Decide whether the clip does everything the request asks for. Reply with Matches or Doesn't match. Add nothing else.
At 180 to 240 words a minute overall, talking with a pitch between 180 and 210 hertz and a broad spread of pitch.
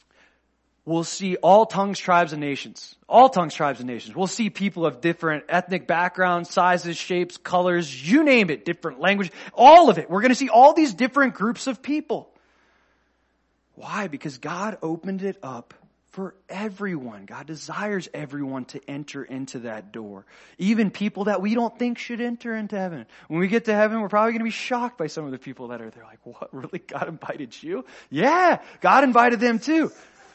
Matches